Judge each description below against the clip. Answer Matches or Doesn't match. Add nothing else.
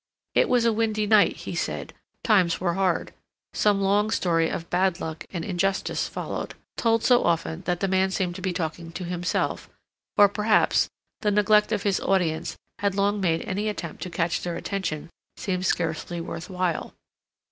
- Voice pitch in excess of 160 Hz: Matches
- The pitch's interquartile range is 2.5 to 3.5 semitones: Matches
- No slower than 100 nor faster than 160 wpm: Doesn't match